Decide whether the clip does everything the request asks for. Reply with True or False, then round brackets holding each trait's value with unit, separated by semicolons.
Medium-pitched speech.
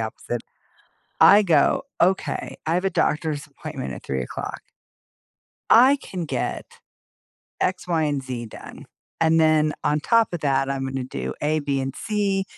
True (155 Hz)